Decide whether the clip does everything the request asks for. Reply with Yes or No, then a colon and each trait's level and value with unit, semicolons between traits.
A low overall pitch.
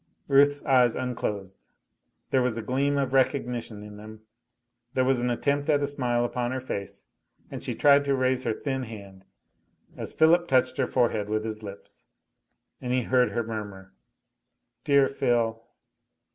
Yes: low, 125 Hz